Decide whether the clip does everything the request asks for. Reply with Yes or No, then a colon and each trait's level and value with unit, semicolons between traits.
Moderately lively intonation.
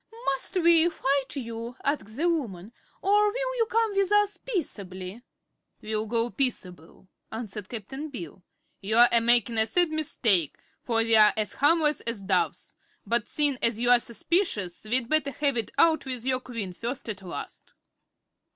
No: wide, 6.2 semitones